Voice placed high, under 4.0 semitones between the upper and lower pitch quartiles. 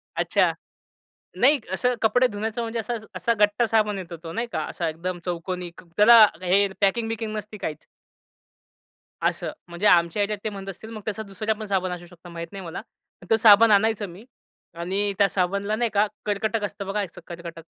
Yes: high, 205 Hz; average, 3.4 semitones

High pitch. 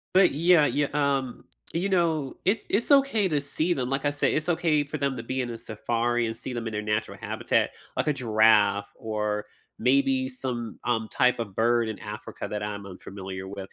No: low, 125 Hz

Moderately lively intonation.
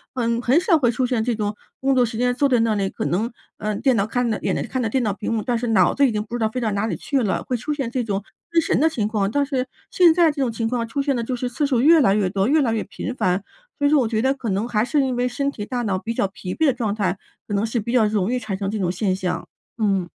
Yes: average, 3.8 semitones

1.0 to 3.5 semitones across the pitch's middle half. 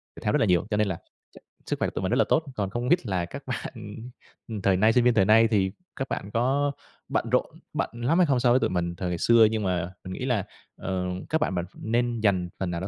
No: average, 4.7 semitones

